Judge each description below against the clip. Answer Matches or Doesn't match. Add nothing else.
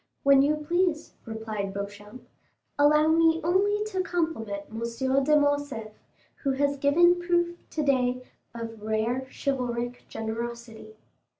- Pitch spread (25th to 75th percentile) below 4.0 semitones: Doesn't match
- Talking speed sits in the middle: Doesn't match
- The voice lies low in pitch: Doesn't match